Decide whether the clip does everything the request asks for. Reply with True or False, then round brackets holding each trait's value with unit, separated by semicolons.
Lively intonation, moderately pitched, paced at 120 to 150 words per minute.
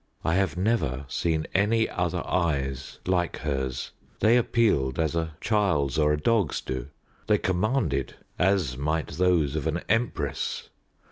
False (5.8 semitones; 85 Hz; 140 wpm)